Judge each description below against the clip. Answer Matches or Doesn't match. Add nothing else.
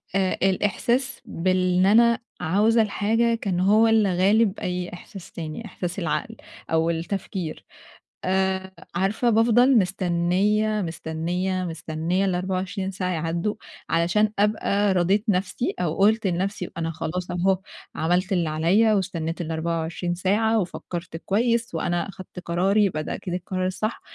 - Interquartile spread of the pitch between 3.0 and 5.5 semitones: Matches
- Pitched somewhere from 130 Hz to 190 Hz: Matches